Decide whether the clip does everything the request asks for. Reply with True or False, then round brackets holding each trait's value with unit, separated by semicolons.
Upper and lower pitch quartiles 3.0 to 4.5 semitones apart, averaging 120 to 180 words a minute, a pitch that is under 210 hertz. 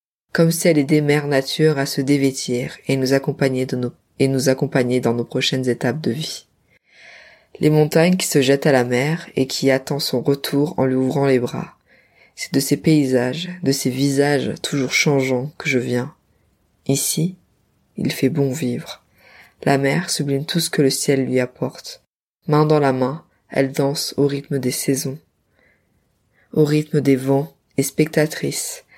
False (2.4 semitones; 175 wpm; 140 Hz)